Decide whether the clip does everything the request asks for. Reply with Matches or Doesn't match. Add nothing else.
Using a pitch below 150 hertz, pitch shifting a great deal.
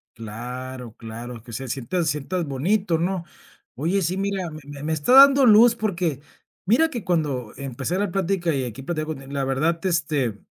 Doesn't match